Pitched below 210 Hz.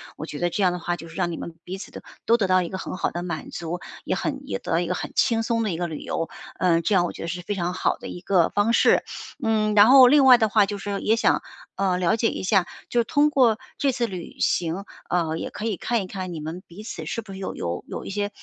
Yes: high, 190 Hz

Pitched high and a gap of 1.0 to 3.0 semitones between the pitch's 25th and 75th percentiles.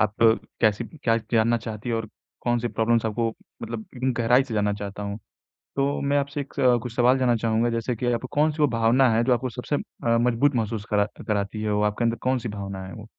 No: low, 115 Hz; narrow, 2.6 semitones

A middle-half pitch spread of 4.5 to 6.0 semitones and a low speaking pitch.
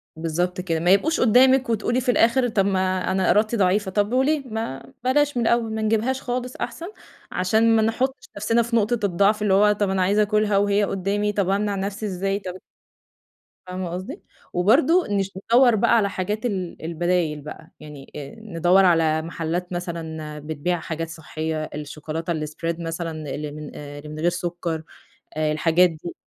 No: average, 4.8 semitones; high, 190 Hz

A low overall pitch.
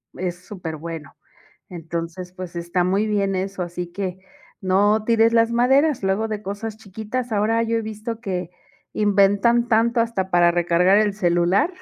No: high, 200 Hz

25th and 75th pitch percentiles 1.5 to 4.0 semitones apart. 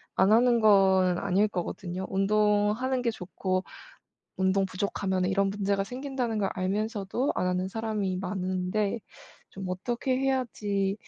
Yes: narrow, 2.6 semitones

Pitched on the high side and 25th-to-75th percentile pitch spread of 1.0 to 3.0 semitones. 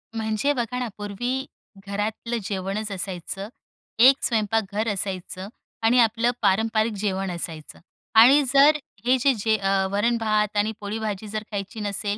Yes: high, 215 Hz; average, 2.7 semitones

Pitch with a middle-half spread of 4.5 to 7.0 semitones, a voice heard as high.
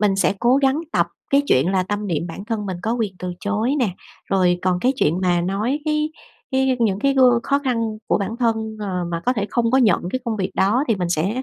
Yes: average, 5.0 semitones; high, 215 Hz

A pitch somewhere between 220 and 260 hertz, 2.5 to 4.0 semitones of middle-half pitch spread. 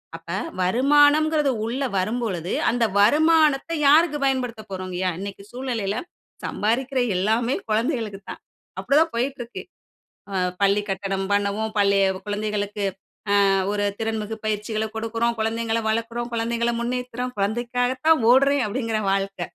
Yes: high, 230 Hz; average, 3.6 semitones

